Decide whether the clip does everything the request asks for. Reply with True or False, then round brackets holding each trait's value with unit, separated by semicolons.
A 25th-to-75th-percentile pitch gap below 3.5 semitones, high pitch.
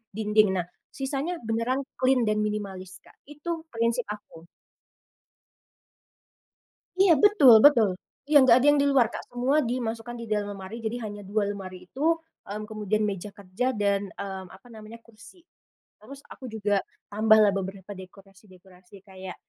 False (3.8 semitones; 215 Hz)